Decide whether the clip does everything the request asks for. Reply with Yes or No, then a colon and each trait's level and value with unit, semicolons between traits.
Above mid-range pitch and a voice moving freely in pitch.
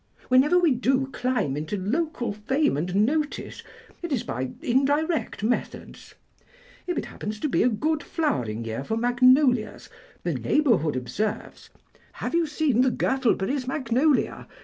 Yes: very high, 255 Hz; wide, 5.8 semitones